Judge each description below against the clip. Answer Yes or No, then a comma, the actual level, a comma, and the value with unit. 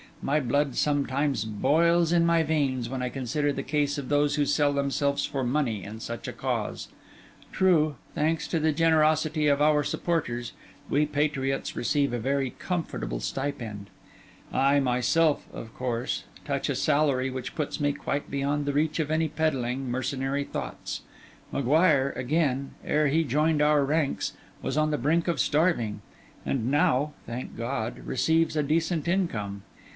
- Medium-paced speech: Yes, average, 155 wpm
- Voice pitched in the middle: Yes, medium, 145 Hz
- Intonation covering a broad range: No, average, 3.0 semitones